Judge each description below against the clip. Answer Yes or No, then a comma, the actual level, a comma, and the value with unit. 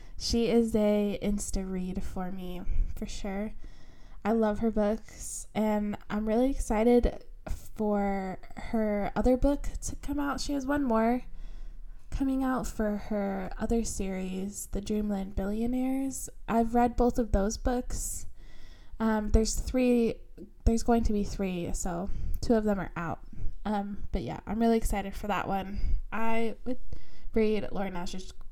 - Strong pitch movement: No, average, 2.8 semitones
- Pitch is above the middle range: Yes, high, 215 Hz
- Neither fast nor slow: Yes, average, 150 wpm